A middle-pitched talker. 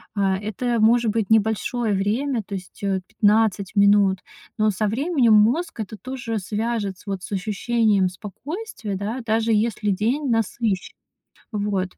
No: high, 215 Hz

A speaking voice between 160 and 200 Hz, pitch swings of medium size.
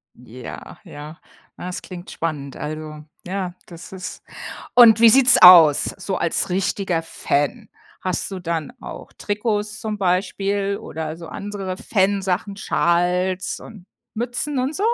Yes: medium, 185 Hz; average, 3.6 semitones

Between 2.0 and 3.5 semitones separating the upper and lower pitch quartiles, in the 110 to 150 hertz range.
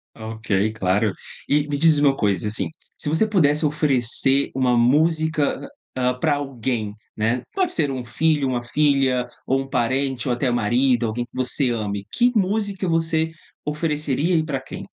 No: average, 4.1 semitones; low, 135 Hz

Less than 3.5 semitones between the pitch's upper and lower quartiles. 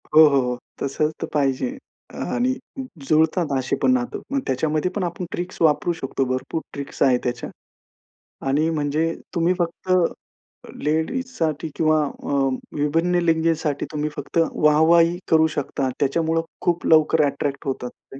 Yes: average, 3.0 semitones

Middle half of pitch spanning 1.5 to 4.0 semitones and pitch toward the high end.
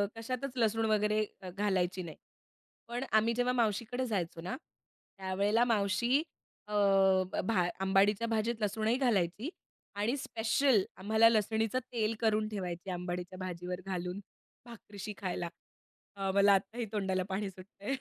Yes: average, 3.3 semitones; high, 210 Hz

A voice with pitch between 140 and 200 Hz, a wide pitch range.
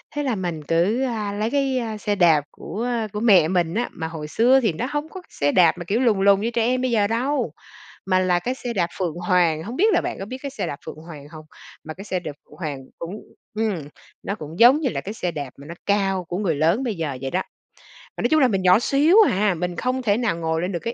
Yes: high, 195 Hz; wide, 6.0 semitones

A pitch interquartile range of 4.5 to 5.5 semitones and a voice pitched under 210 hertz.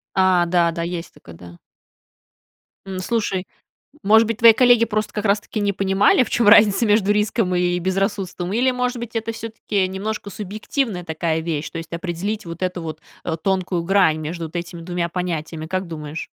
No: average, 3.8 semitones; medium, 185 Hz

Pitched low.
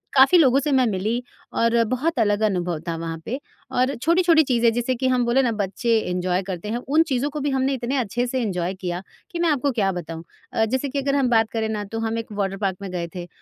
No: high, 235 Hz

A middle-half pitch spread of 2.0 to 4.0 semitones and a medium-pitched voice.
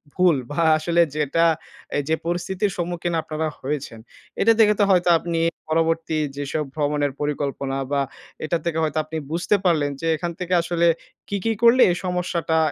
Yes: average, 2.7 semitones; medium, 165 Hz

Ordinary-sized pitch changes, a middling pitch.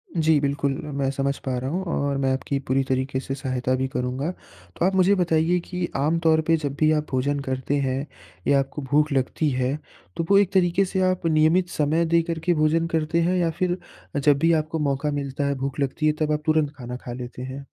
Yes: average, 3.6 semitones; medium, 150 Hz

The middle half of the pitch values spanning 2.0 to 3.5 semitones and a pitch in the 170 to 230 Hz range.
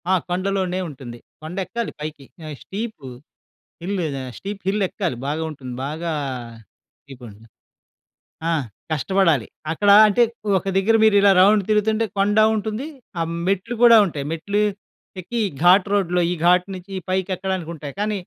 No: average, 3.9 semitones; high, 190 Hz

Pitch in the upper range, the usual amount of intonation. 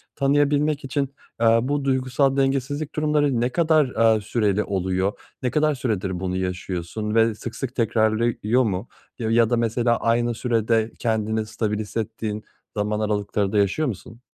No: low, 115 Hz; average, 3.7 semitones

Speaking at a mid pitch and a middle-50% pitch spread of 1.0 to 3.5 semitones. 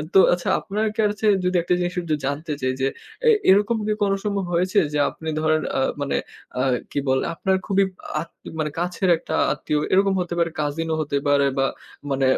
No: medium, 170 Hz; average, 4.6 semitones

